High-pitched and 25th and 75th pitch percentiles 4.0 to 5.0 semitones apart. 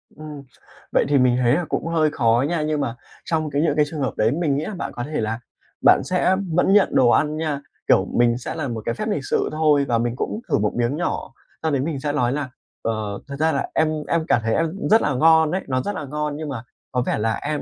No: medium, 145 Hz; average, 4.4 semitones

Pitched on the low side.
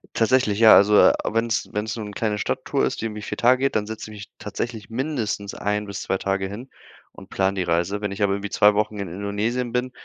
Yes: low, 105 Hz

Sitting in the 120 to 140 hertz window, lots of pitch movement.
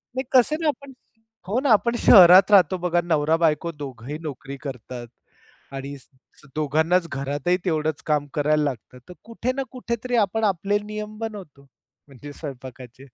No: medium, 160 Hz; wide, 6.8 semitones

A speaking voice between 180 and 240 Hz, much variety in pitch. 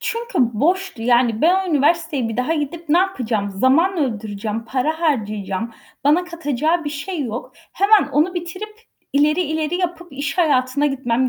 No: very high, 295 Hz; wide, 5.9 semitones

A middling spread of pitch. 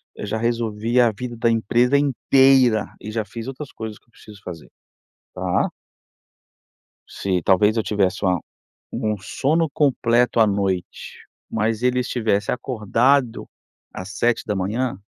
Yes: average, 3.3 semitones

